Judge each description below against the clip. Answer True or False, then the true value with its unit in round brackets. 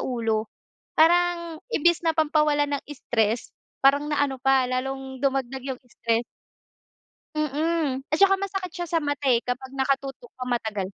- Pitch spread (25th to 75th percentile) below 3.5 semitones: False (3.8 semitones)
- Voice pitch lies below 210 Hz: False (275 Hz)